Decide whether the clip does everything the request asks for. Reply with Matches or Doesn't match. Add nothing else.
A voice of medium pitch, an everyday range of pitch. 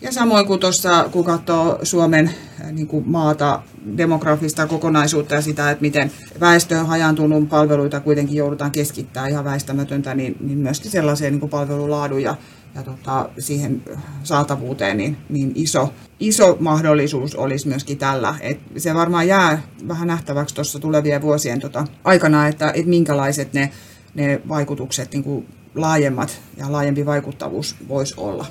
Doesn't match